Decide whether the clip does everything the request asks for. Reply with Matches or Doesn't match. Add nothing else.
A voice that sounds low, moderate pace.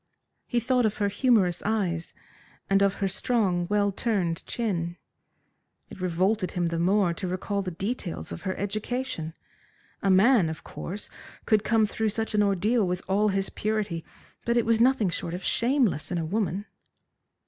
Doesn't match